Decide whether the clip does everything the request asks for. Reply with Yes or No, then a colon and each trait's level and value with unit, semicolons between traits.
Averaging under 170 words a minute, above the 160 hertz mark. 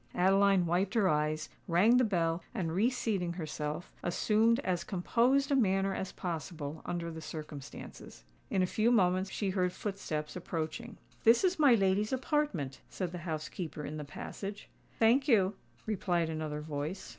Yes: average, 155 wpm; medium, 185 Hz